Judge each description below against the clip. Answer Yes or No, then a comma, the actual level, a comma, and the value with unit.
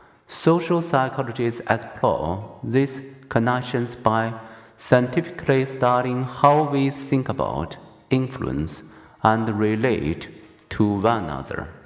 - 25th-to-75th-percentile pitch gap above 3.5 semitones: No, average, 3.2 semitones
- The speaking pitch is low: Yes, low, 125 Hz